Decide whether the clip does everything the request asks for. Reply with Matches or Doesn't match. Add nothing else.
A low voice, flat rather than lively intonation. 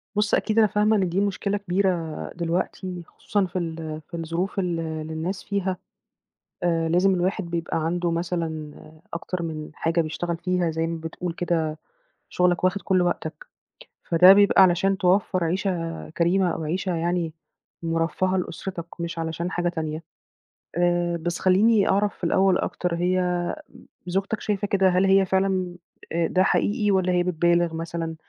Doesn't match